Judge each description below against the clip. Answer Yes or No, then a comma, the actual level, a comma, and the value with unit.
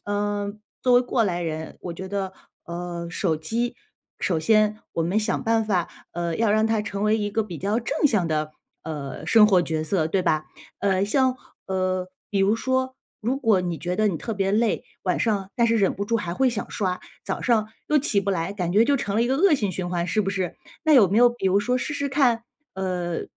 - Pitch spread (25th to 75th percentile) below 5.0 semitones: Yes, average, 4.1 semitones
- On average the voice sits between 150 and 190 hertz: No, high, 200 Hz